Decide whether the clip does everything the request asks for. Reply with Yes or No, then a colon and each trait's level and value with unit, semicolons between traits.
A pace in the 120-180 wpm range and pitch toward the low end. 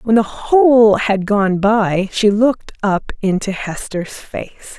No: average, 150 wpm; high, 210 Hz